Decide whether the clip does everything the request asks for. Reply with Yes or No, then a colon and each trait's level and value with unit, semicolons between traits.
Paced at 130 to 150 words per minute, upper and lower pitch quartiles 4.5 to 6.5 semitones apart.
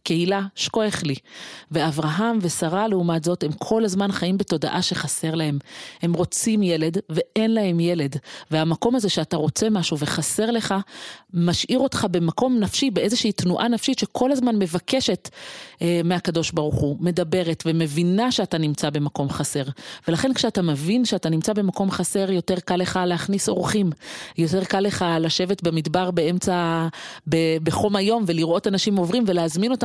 No: average, 145 wpm; average, 4.1 semitones